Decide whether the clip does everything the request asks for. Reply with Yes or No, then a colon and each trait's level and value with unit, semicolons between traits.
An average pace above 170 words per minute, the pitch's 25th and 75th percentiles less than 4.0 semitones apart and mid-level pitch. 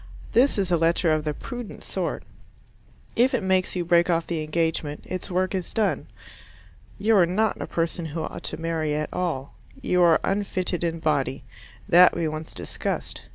Yes: average, 180 wpm; average, 2.7 semitones; medium, 170 Hz